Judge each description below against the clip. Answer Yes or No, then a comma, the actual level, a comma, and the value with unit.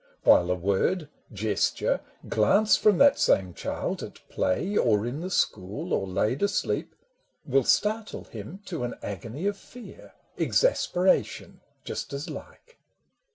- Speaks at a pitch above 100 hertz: Yes, low, 135 Hz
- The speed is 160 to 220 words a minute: No, slow, 135 wpm